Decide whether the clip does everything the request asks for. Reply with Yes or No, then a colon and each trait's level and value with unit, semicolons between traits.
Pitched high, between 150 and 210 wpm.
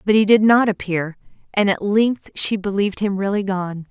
Yes: high, 200 Hz; average, 200 wpm